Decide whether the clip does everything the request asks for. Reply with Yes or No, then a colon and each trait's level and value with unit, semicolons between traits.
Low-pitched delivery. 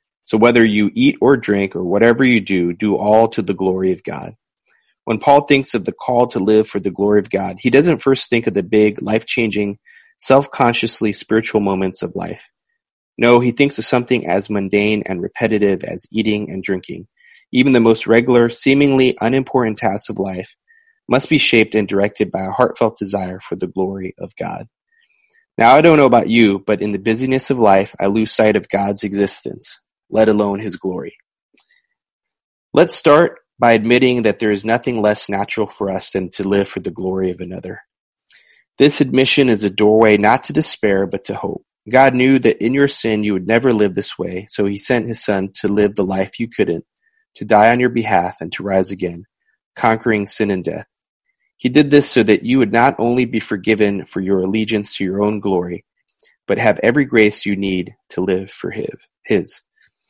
Yes: low, 110 Hz